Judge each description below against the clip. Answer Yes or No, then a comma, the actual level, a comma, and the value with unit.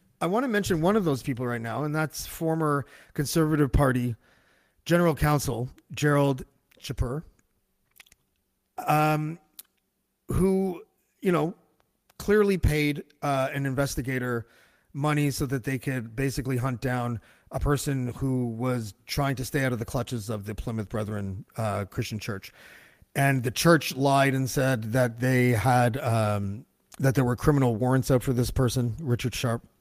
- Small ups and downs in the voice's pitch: No, average, 3.4 semitones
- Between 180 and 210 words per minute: No, average, 150 wpm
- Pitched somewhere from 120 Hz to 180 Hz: Yes, low, 135 Hz